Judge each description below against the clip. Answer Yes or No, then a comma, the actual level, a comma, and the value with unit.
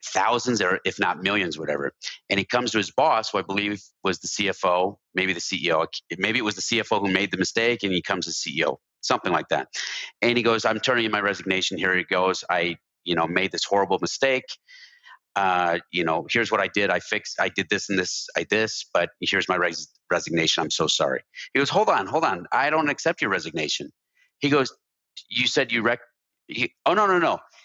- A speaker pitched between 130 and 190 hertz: No, low, 100 Hz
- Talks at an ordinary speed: No, fast, 220 wpm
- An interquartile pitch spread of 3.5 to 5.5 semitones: Yes, average, 4.1 semitones